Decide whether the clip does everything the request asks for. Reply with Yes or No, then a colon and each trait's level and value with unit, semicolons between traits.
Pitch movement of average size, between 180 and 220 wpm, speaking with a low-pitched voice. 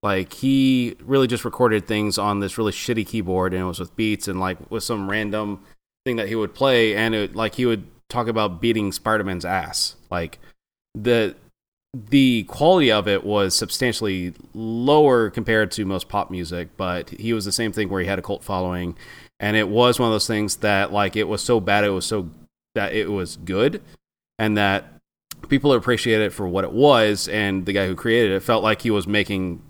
Yes: average, 3.0 semitones; fast, 205 wpm; low, 105 Hz